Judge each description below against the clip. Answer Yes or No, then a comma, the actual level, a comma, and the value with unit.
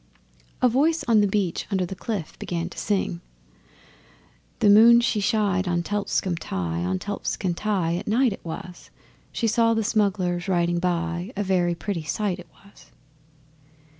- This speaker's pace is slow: No, average, 160 wpm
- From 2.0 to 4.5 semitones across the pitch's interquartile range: Yes, average, 3.6 semitones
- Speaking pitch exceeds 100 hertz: Yes, high, 190 Hz